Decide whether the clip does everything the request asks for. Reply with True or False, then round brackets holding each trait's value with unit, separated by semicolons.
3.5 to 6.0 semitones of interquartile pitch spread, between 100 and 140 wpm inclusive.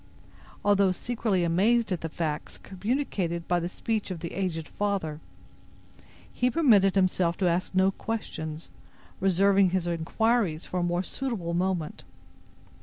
False (3.1 semitones; 135 wpm)